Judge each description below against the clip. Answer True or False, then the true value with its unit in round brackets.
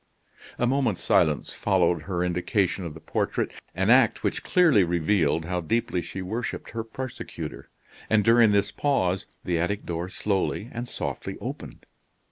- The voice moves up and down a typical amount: True (4.7 semitones)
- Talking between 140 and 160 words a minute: True (150 wpm)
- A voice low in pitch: True (95 Hz)